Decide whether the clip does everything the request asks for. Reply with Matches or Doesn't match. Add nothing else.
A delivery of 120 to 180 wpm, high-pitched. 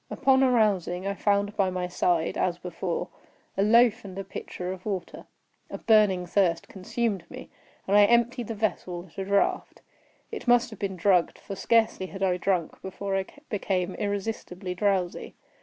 Matches